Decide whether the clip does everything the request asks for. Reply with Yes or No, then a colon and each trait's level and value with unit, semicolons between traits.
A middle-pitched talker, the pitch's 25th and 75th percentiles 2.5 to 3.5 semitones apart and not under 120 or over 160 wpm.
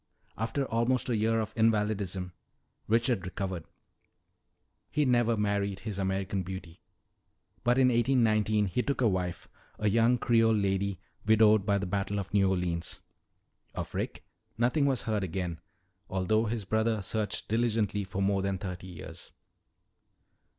No: low, 105 Hz; average, 3.0 semitones; average, 140 wpm